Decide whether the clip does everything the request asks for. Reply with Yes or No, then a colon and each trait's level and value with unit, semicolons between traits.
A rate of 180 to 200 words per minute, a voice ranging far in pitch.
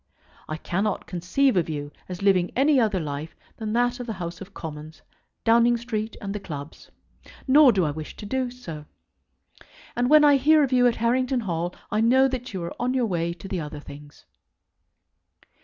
Yes: average, 190 wpm; wide, 6.7 semitones